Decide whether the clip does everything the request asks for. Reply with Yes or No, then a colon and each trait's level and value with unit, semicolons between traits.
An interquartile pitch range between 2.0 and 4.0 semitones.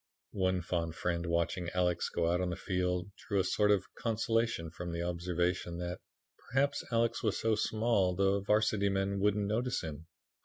Yes: average, 3.3 semitones